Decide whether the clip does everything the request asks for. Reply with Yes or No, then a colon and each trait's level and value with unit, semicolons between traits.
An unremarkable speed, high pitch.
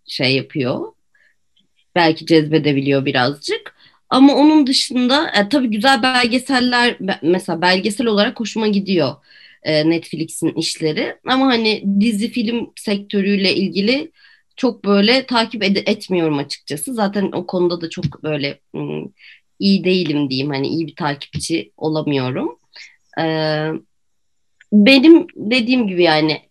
Yes: average, 110 wpm; high, 195 Hz